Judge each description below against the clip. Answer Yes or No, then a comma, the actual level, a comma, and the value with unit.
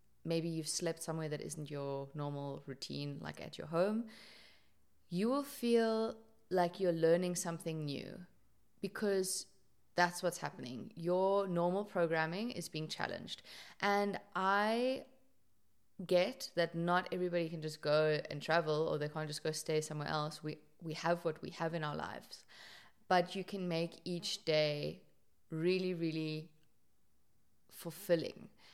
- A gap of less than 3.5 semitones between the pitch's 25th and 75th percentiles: Yes, average, 3.1 semitones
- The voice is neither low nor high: Yes, medium, 170 Hz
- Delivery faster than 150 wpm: No, average, 140 wpm